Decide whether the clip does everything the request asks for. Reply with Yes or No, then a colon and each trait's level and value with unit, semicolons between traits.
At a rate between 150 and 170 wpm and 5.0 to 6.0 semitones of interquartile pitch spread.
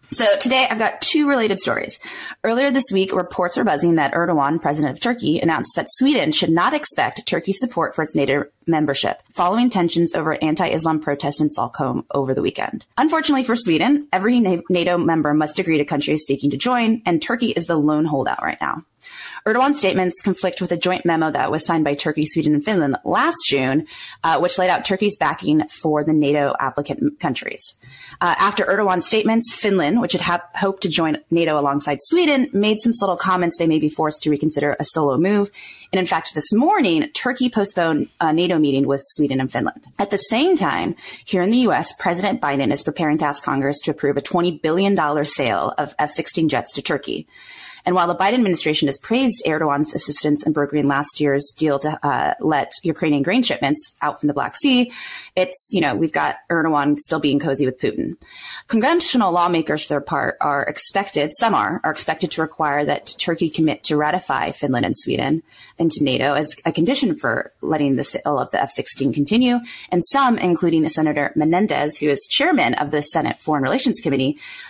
No: average, 195 wpm; wide, 5.6 semitones